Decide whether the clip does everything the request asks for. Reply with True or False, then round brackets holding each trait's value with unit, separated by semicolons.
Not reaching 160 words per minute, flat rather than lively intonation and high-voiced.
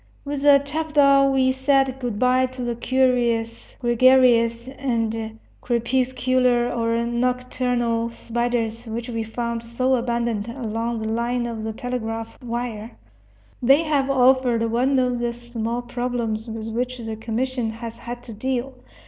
True (140 wpm; 2.0 semitones; 240 Hz)